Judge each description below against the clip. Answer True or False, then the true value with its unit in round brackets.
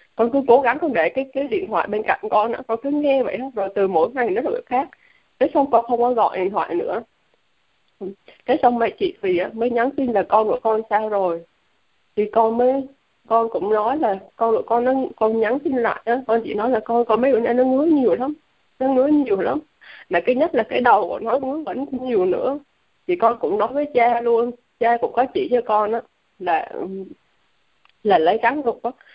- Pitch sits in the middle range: False (240 Hz)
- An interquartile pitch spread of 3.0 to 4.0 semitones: True (3.5 semitones)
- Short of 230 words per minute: False (235 wpm)